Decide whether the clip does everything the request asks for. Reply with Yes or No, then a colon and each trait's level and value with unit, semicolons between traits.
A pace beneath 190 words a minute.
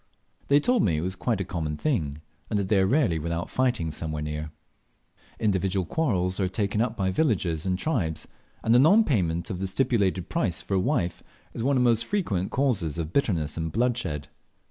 No: average, 195 wpm